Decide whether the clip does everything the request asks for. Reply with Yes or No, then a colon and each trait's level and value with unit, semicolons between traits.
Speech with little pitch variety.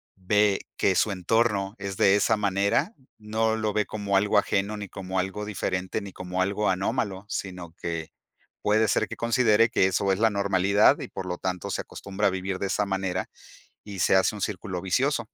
Yes: narrow, 2.1 semitones